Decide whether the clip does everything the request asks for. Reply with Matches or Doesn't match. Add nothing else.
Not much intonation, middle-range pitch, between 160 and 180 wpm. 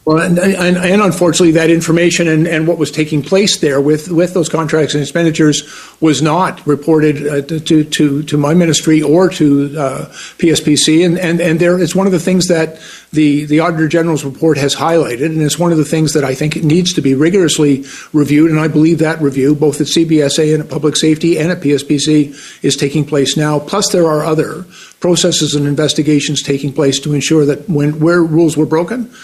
Doesn't match